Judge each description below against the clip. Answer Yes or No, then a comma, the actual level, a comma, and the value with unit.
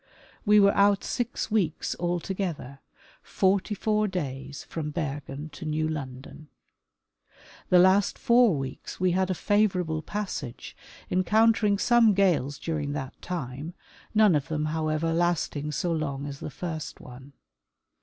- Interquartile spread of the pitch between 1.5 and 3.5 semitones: No, average, 5.2 semitones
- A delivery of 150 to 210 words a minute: No, slow, 135 wpm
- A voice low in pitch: No, medium, 165 Hz